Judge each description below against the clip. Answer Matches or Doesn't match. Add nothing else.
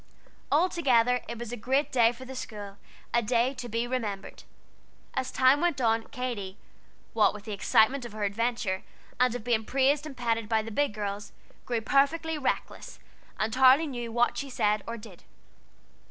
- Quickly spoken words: Doesn't match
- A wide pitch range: Doesn't match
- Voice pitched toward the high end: Matches